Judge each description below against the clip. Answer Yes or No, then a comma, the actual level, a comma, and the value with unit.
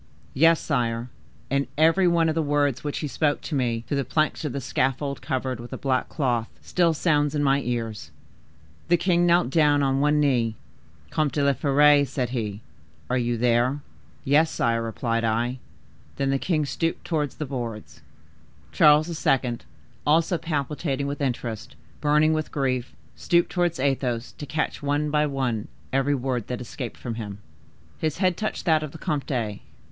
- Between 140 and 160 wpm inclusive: No, average, 175 wpm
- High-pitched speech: No, medium, 140 Hz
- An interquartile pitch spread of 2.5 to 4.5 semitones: Yes, average, 3.7 semitones